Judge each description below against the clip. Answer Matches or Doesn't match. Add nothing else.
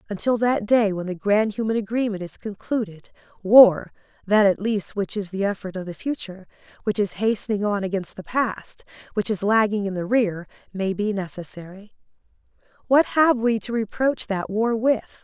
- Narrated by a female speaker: Matches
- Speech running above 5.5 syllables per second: Doesn't match